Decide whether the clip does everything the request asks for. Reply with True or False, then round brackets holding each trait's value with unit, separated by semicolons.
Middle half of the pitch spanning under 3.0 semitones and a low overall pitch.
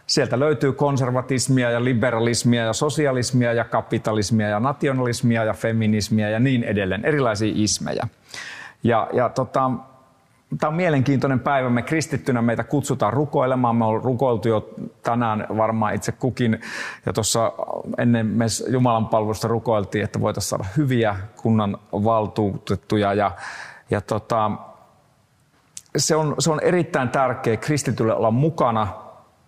False (3.4 semitones; 120 Hz)